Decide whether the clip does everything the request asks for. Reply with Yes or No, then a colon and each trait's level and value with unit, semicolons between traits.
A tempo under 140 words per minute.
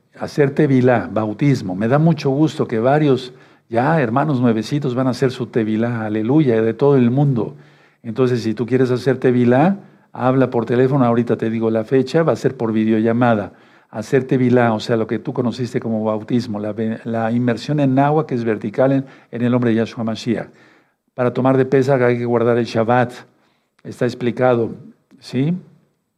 No: average, 180 wpm